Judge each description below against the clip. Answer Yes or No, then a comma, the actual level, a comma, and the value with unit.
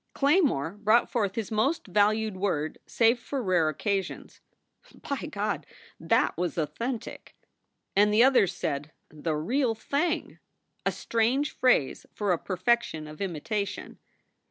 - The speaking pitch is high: Yes, high, 210 Hz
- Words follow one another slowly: Yes, slow, 130 wpm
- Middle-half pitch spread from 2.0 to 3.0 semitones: No, wide, 5.6 semitones